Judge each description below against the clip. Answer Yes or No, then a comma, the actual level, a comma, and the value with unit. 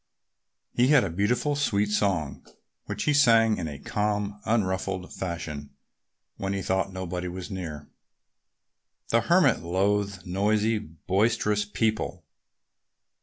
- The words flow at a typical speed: No, slow, 120 wpm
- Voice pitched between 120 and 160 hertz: No, low, 100 Hz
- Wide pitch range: No, average, 2.8 semitones